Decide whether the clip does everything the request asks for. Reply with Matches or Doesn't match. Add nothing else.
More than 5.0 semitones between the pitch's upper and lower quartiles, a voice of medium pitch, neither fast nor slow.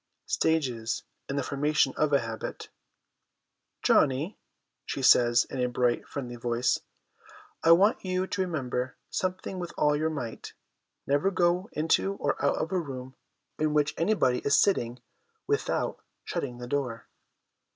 Matches